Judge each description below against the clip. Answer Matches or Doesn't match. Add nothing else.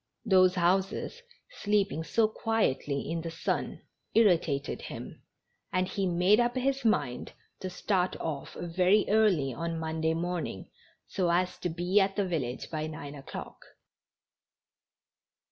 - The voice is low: Doesn't match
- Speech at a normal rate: Doesn't match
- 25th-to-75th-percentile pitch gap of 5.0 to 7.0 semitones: Doesn't match